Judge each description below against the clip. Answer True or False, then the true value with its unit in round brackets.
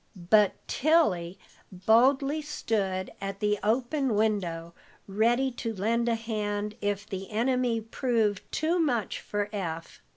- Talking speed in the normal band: False (125 wpm)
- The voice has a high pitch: True (215 Hz)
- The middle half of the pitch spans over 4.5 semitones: False (3.7 semitones)